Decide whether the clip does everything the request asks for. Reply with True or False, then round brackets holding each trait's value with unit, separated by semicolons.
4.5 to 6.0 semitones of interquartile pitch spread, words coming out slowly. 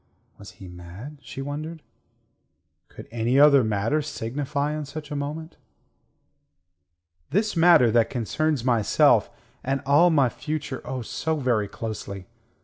True (4.8 semitones; 130 wpm)